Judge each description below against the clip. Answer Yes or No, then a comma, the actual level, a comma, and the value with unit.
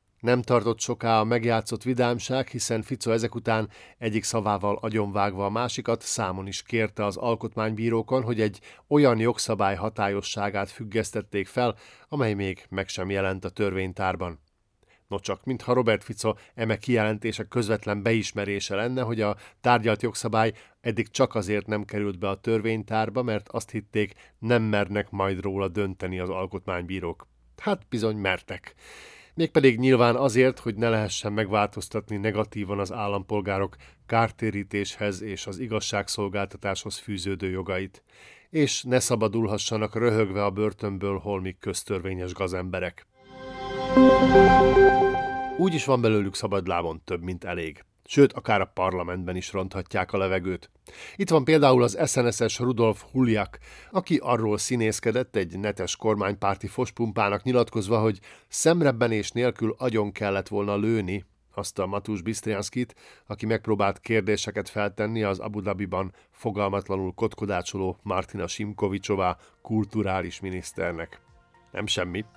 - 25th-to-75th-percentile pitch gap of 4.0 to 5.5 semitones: No, average, 3.0 semitones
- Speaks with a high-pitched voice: No, low, 105 Hz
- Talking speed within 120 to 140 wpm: Yes, average, 125 wpm